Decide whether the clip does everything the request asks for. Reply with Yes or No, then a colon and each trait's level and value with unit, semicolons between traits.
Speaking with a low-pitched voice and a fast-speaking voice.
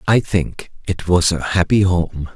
No: very low, 90 Hz; average, 180 wpm